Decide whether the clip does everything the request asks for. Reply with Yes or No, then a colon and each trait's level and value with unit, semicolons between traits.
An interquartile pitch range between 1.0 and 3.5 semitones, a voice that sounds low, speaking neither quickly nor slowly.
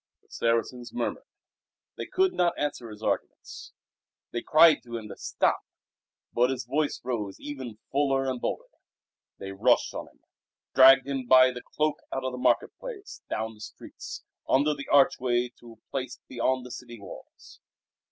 Yes: average, 2.9 semitones; low, 130 Hz; average, 165 wpm